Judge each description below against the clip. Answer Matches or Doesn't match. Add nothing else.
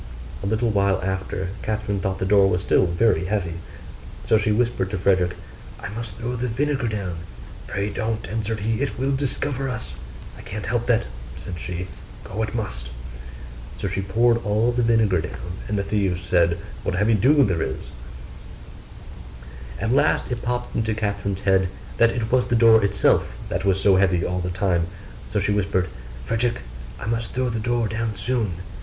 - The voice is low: Matches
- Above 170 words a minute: Matches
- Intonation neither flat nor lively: Matches